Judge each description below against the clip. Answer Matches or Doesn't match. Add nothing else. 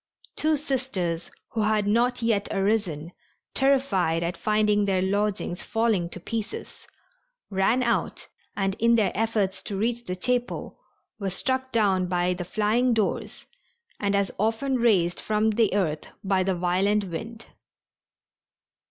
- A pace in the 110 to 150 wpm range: Matches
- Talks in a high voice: Matches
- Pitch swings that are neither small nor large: Matches